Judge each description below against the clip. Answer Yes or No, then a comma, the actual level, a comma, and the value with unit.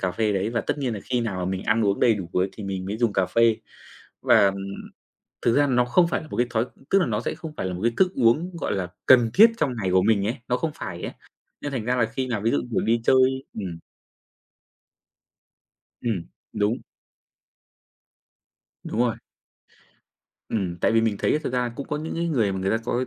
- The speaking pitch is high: No, low, 115 Hz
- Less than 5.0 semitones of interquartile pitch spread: Yes, average, 4.6 semitones